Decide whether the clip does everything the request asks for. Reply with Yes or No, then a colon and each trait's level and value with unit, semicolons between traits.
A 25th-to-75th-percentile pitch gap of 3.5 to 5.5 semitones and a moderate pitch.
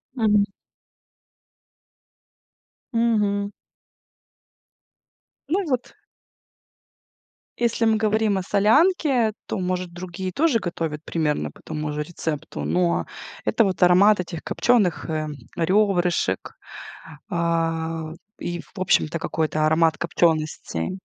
Yes: average, 4.8 semitones; medium, 180 Hz